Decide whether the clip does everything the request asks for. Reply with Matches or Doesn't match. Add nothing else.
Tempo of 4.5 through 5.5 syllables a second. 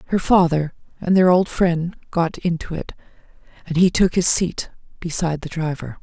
Matches